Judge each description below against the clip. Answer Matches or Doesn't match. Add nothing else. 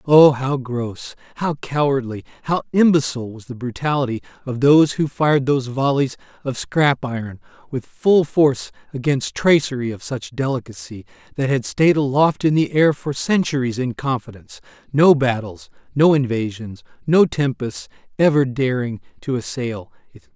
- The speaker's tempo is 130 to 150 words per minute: Matches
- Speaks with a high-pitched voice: Doesn't match